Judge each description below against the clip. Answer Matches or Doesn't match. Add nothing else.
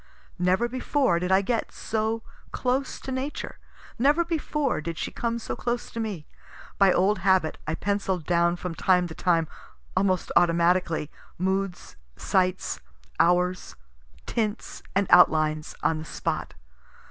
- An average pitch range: Matches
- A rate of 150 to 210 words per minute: Doesn't match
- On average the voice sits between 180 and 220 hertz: Matches